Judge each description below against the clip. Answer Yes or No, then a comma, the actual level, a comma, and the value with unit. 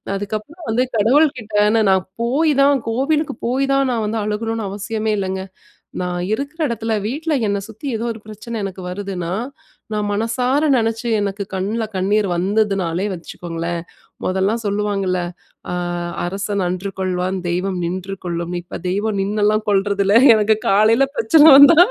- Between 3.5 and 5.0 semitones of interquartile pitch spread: No, average, 3.1 semitones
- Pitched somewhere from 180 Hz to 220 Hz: Yes, high, 210 Hz